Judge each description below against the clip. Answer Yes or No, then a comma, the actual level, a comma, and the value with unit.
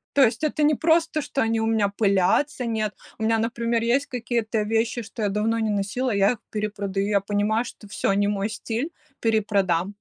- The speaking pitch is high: Yes, high, 220 Hz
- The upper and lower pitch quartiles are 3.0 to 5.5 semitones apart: No, narrow, 2.5 semitones